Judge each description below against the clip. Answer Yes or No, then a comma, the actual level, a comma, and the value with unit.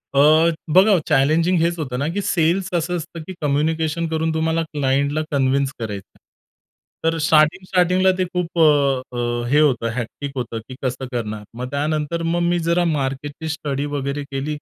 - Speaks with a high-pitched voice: No, medium, 155 Hz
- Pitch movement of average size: Yes, average, 3.7 semitones